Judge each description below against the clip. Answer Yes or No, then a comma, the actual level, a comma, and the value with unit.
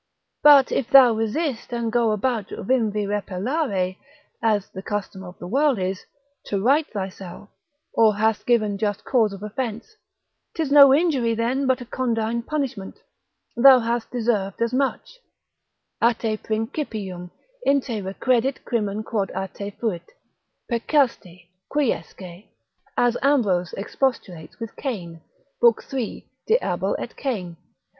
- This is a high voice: Yes, high, 225 Hz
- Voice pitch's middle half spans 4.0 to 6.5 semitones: Yes, average, 4.7 semitones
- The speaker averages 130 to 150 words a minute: Yes, slow, 135 wpm